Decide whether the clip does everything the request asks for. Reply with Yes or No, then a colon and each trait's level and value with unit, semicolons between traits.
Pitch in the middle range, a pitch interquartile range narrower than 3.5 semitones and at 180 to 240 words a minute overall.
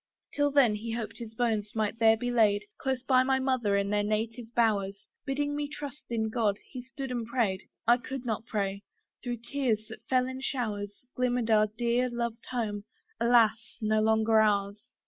No: high, 230 Hz; average, 2.8 semitones; average, 185 wpm